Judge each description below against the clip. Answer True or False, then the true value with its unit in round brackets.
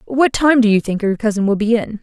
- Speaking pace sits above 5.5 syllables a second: True (5.8 syllables/s)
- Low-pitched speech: False (225 Hz)